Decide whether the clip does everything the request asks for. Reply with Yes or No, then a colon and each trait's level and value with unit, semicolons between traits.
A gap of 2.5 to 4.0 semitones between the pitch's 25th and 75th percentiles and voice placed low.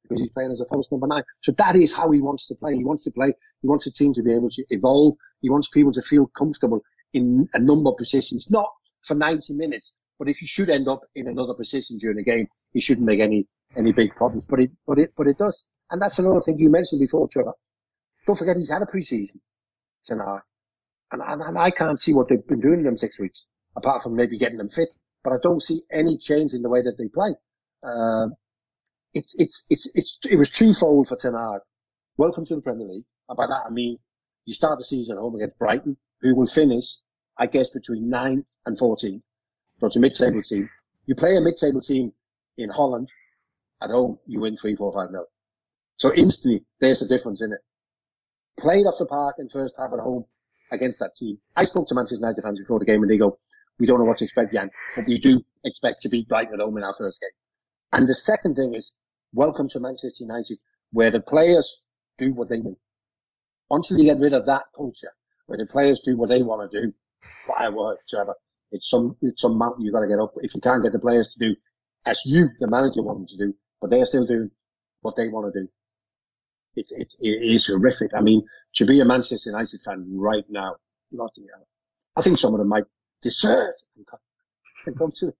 No: average, 4.7 semitones; low, 125 Hz